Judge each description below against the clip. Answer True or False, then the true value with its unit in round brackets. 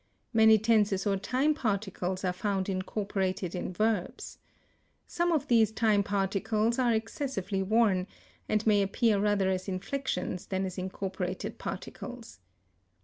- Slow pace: True (130 wpm)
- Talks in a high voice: True (200 Hz)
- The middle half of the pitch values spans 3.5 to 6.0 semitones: False (2.8 semitones)